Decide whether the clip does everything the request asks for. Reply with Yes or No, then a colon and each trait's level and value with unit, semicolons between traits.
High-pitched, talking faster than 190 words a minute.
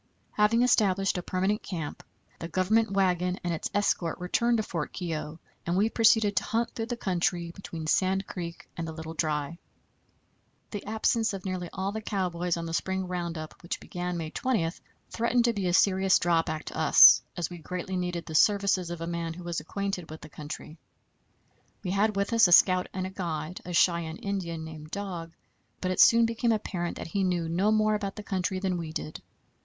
No: medium, 180 Hz; average, 200 wpm